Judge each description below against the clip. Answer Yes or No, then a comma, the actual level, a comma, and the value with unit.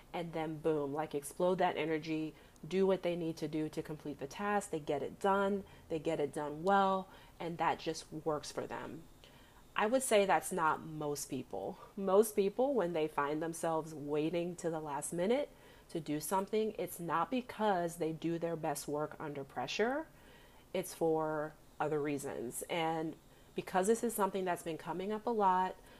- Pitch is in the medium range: Yes, medium, 165 Hz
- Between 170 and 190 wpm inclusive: Yes, average, 180 wpm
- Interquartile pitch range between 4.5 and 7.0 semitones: No, average, 3.7 semitones